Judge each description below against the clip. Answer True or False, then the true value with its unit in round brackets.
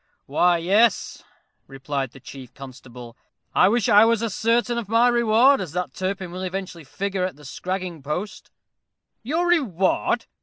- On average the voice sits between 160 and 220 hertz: True (190 Hz)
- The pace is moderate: True (155 wpm)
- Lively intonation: True (6.7 semitones)